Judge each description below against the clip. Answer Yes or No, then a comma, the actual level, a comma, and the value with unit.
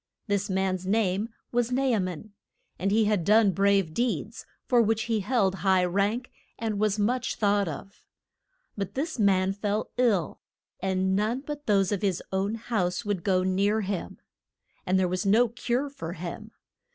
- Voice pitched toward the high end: Yes, high, 205 Hz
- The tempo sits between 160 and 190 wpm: Yes, average, 170 wpm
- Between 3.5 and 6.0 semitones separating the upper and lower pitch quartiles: No, average, 3.0 semitones